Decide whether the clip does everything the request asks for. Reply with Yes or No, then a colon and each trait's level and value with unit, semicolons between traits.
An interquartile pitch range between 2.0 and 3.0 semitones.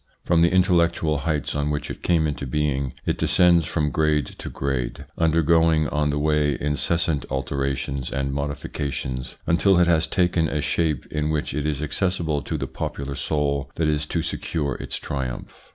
Yes: narrow, 2.6 semitones